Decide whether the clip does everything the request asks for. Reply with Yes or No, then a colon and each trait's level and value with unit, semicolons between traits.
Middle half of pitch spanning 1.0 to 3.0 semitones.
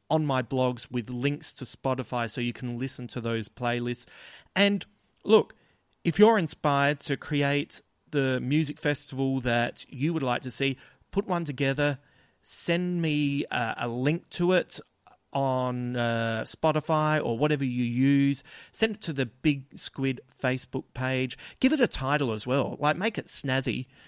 No: average, 3.4 semitones